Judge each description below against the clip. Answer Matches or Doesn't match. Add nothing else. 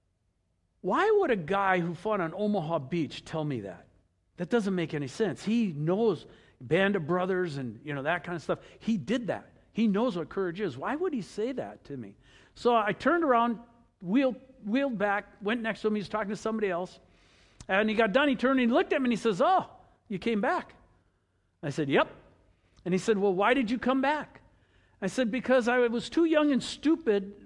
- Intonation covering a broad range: Matches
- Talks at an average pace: Doesn't match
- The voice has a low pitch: Doesn't match